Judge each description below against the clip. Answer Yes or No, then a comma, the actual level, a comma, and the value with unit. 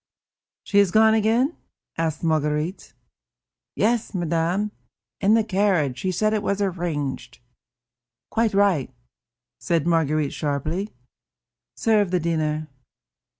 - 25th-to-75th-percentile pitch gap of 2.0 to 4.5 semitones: No, average, 5.1 semitones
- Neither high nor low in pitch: Yes, medium, 175 Hz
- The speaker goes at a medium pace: No, slow, 110 wpm